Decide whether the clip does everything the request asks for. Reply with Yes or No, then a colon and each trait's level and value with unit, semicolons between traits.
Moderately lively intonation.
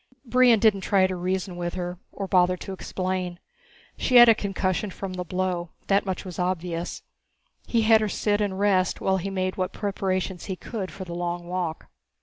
No: narrow, 1.9 semitones